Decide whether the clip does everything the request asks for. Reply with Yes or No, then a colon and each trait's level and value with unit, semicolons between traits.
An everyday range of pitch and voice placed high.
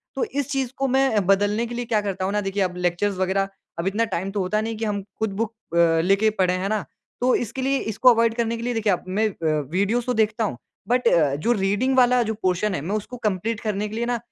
Yes: average, 3.4 semitones; high, 215 Hz